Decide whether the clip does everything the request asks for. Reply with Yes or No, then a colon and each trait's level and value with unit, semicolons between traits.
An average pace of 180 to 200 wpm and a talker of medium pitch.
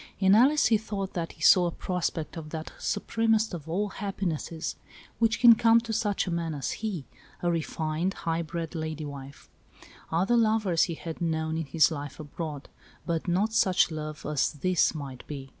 Yes: average, 185 wpm; medium, 170 Hz